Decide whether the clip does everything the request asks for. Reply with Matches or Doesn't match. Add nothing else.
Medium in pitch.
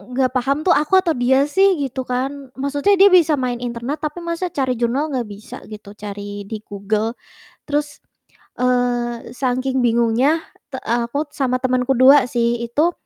Doesn't match